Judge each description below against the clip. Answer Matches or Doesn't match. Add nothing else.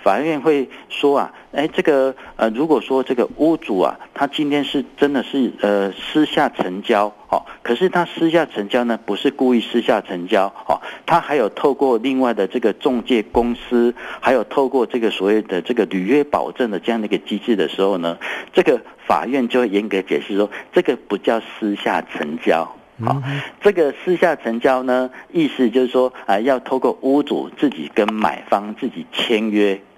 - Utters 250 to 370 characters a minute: Matches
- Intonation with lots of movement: Doesn't match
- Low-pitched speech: Matches